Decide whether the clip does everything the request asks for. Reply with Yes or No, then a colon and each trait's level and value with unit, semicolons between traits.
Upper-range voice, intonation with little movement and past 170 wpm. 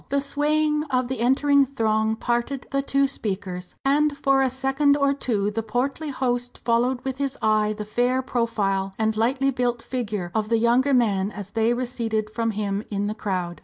No: high, 240 Hz; average, 4.1 semitones; average, 185 wpm